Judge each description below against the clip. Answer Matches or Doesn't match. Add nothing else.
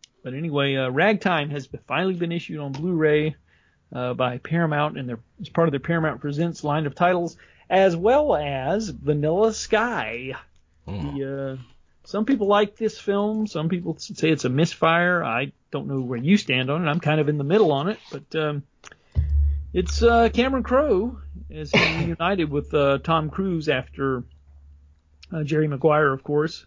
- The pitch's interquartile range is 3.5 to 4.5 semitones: Doesn't match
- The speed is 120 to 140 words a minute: Doesn't match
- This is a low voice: Doesn't match